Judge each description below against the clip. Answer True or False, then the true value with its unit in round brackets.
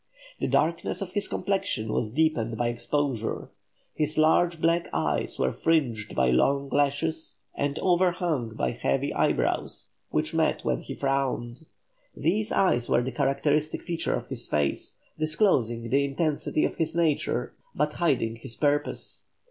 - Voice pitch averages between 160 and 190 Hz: False (145 Hz)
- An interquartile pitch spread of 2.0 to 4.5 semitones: False (5.5 semitones)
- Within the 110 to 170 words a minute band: True (145 wpm)